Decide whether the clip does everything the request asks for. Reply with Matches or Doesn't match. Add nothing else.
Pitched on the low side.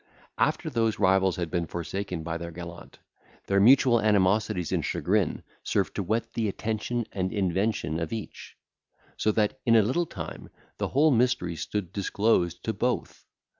Matches